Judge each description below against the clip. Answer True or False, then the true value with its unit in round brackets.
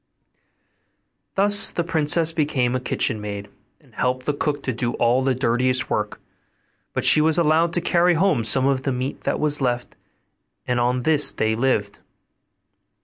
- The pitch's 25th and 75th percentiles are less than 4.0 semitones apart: False (4.3 semitones)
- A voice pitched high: False (130 Hz)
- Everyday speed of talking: True (165 wpm)